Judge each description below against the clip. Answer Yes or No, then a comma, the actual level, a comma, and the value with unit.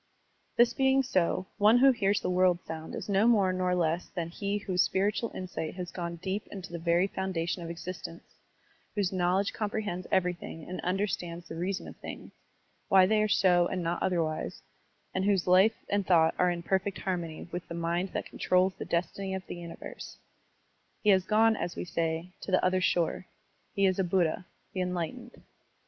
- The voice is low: No, medium, 185 Hz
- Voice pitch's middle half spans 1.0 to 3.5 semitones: Yes, narrow, 2.5 semitones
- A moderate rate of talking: Yes, average, 190 wpm